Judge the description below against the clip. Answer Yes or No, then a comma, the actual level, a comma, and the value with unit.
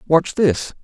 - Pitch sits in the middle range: Yes, medium, 160 Hz